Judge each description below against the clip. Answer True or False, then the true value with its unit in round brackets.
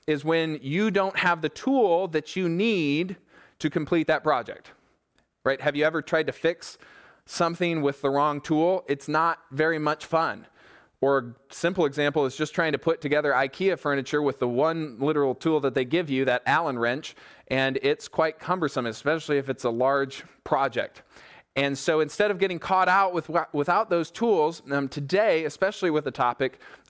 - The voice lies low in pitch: False (155 Hz)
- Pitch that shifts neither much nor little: True (3.4 semitones)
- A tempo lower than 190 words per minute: True (180 wpm)